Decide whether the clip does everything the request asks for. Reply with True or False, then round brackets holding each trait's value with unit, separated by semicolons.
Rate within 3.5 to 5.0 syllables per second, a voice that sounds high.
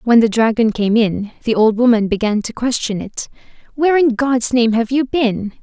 True (4.9 syllables/s; 230 Hz)